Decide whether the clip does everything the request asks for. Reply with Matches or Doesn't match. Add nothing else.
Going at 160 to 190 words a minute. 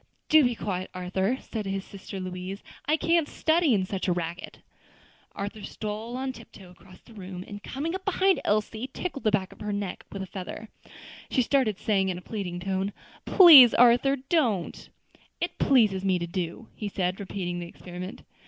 Matches